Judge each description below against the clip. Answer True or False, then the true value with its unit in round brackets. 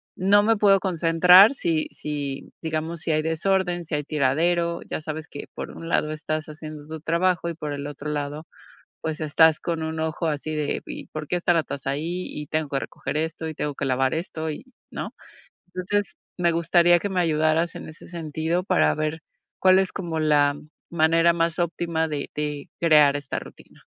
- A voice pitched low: False (160 Hz)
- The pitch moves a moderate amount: False (2.2 semitones)